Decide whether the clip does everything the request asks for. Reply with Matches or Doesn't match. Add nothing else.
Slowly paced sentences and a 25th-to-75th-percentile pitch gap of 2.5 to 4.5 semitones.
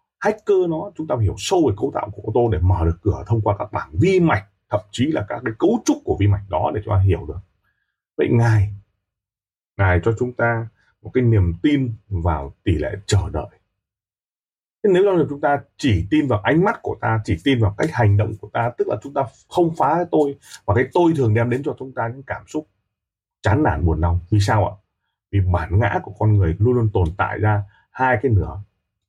Doesn't match